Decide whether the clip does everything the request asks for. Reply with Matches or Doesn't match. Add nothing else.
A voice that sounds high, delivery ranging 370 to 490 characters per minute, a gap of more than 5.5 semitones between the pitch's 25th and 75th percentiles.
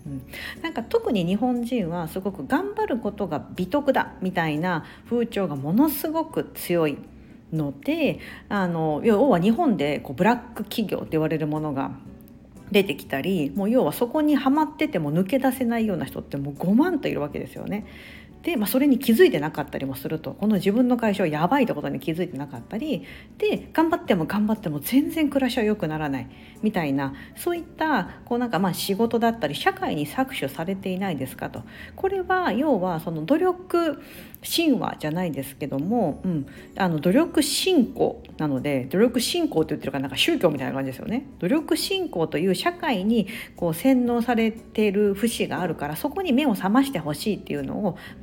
Matches